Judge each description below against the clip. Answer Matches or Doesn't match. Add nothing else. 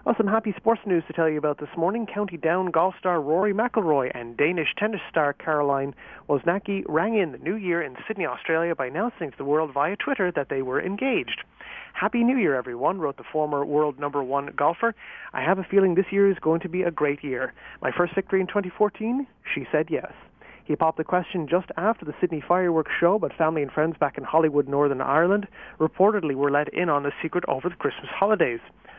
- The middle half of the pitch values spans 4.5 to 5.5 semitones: Matches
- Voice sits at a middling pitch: Matches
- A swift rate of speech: Matches